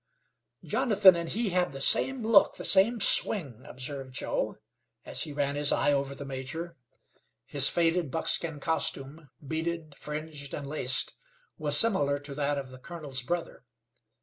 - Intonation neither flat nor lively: Yes, average, 3.7 semitones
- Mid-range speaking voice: Yes, medium, 150 Hz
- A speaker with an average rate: Yes, average, 150 wpm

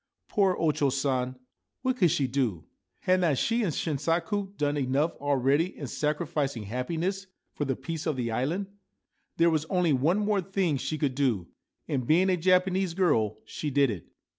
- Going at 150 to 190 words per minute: Yes, average, 175 wpm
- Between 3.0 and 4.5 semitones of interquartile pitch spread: No, average, 5.3 semitones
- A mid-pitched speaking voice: Yes, medium, 150 Hz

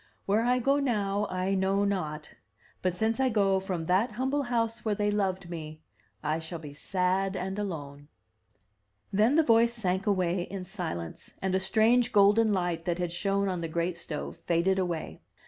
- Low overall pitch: No, high, 190 Hz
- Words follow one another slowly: No, average, 180 wpm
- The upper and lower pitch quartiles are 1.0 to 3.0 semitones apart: No, average, 3.6 semitones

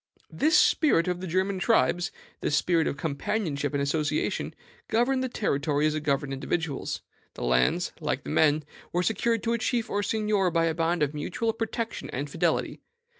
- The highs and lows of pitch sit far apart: Yes, wide, 6.9 semitones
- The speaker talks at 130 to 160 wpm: No, average, 175 wpm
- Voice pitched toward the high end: No, medium, 170 Hz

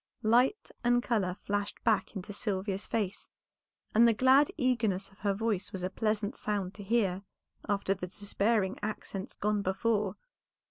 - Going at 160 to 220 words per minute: No, average, 150 wpm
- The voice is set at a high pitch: Yes, high, 205 Hz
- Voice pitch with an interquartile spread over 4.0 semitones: No, average, 2.9 semitones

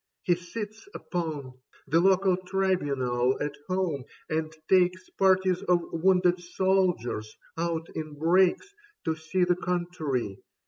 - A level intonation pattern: No, average, 3.2 semitones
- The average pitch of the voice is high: No, medium, 175 Hz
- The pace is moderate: No, slow, 120 wpm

